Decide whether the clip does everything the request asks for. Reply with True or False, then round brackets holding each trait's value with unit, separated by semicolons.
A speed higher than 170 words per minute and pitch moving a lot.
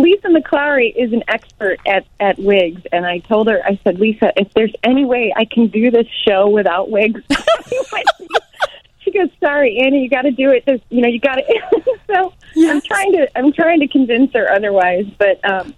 True (200 wpm; 7.0 semitones)